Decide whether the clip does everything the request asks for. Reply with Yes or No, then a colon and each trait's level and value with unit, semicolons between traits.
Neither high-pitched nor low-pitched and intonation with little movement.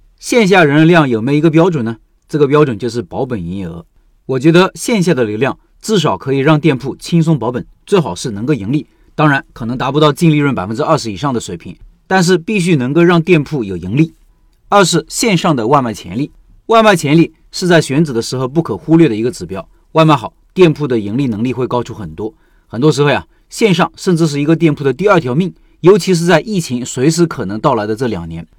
No: medium, 150 Hz; wide, 5.6 semitones